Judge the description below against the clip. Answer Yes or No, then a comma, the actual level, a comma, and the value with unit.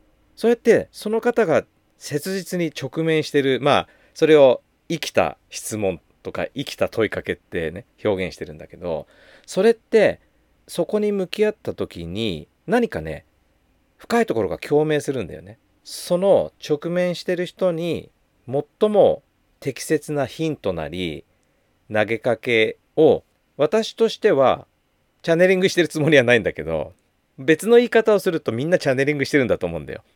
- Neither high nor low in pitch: Yes, medium, 150 Hz